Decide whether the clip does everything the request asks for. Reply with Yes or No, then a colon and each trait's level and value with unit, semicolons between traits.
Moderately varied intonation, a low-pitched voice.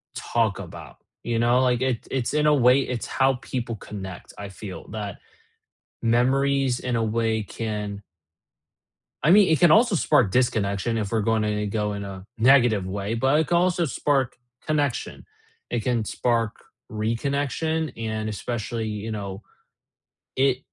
Yes: average, 4.2 semitones; low, 115 Hz